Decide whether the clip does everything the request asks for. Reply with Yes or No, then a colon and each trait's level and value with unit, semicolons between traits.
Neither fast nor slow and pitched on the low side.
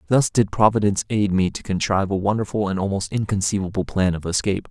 Yes: average, 190 wpm; low, 100 Hz